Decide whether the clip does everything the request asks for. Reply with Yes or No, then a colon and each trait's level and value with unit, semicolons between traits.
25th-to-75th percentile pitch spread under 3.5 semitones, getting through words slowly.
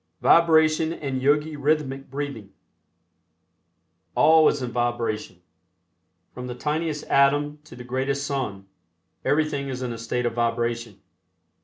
No: average, 3.8 semitones; slow, 125 wpm